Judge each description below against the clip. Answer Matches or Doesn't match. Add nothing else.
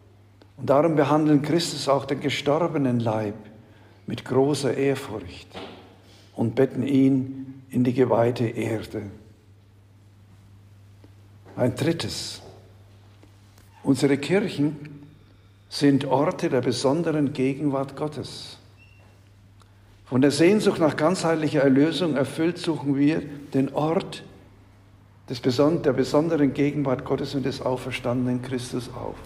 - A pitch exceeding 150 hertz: Doesn't match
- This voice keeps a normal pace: Doesn't match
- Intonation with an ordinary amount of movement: Doesn't match